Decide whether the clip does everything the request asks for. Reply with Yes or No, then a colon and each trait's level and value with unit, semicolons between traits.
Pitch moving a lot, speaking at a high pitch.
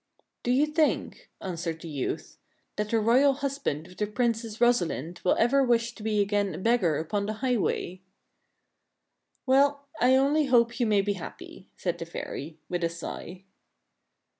Yes: wide, 5.8 semitones; high, 220 Hz